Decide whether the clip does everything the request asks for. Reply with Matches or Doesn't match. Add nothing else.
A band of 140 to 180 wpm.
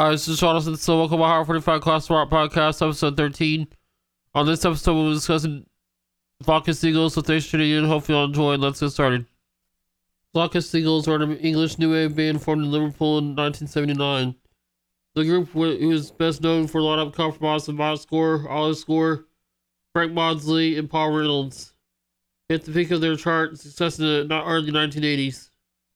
Doesn't match